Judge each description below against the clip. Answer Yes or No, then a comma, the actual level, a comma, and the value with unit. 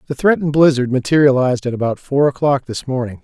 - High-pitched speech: No, low, 135 Hz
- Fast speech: No, average, 185 wpm